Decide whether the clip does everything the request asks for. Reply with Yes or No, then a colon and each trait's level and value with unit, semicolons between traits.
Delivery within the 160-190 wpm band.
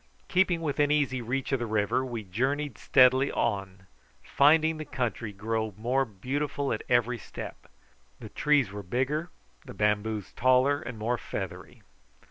No: average, 145 wpm